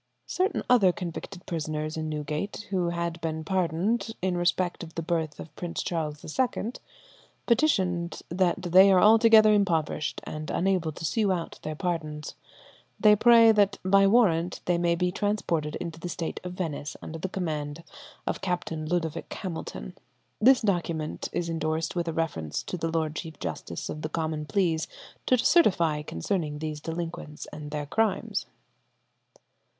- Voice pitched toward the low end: No, medium, 170 Hz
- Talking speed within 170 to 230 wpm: No, average, 155 wpm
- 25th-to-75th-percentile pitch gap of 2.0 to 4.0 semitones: Yes, average, 3.5 semitones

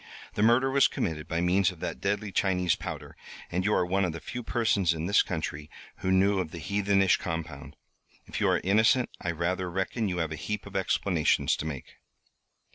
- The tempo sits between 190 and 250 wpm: Yes, average, 200 wpm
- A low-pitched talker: Yes, very low, 95 Hz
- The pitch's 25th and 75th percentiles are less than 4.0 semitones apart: Yes, average, 3.4 semitones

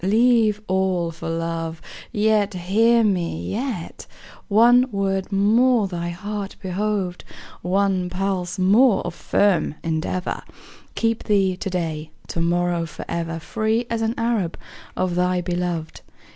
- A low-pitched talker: No, high, 190 Hz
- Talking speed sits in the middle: No, slow, 125 wpm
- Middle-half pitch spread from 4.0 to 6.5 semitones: No, average, 3.6 semitones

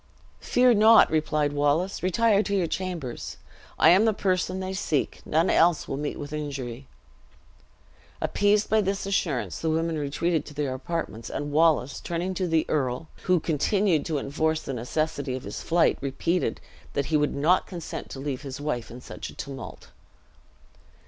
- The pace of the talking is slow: No, average, 170 wpm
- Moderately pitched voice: Yes, medium, 155 Hz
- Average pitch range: Yes, average, 4.5 semitones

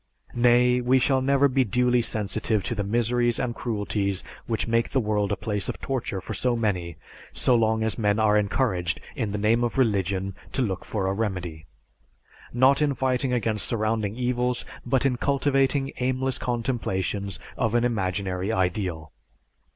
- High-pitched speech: No, low, 115 Hz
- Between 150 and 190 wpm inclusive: Yes, average, 165 wpm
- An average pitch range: Yes, average, 3.7 semitones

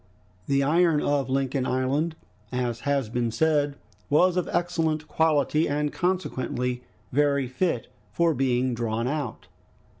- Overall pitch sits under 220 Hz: Yes, medium, 140 Hz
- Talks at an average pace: No, slow, 125 wpm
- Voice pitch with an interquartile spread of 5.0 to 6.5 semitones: No, average, 3.9 semitones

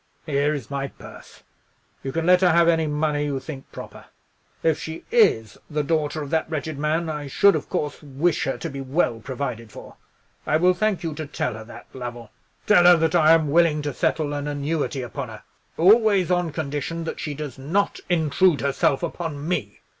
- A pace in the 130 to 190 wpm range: No, average, 200 wpm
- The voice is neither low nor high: Yes, medium, 155 Hz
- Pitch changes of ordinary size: Yes, average, 3.1 semitones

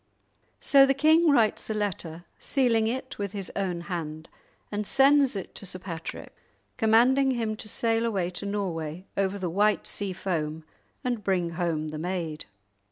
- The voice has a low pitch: No, high, 200 Hz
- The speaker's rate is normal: Yes, average, 165 wpm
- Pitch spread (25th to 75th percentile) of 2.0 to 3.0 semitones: No, average, 4.9 semitones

